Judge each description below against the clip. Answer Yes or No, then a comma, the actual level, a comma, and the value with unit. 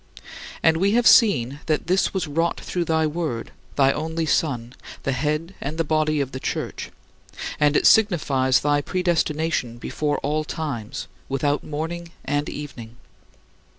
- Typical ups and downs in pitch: Yes, average, 3.0 semitones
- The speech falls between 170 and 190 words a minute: No, average, 150 wpm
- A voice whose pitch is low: No, medium, 150 Hz